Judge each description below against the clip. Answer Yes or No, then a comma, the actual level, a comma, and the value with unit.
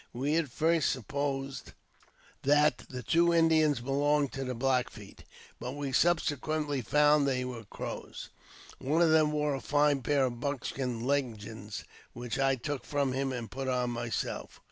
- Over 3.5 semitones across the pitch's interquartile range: No, average, 2.8 semitones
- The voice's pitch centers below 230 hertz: Yes, low, 135 Hz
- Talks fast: No, average, 160 wpm